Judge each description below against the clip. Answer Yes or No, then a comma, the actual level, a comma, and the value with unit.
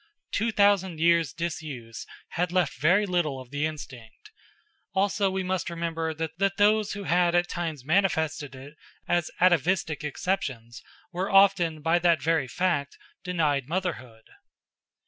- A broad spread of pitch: No, average, 4.0 semitones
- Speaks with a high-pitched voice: No, medium, 170 Hz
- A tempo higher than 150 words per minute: No, slow, 135 wpm